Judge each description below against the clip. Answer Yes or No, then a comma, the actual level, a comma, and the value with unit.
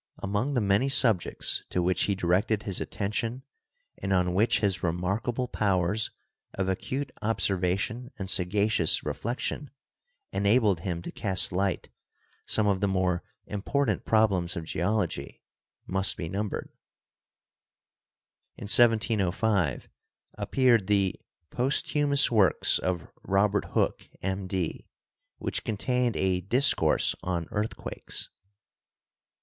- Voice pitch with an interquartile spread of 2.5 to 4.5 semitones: Yes, average, 3.5 semitones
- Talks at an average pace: No, slow, 110 wpm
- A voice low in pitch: Yes, low, 100 Hz